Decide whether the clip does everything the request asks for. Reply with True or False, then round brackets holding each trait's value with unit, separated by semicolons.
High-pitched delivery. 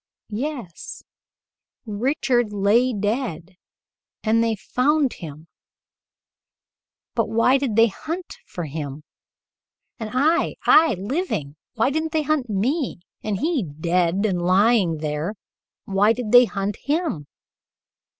True (220 Hz)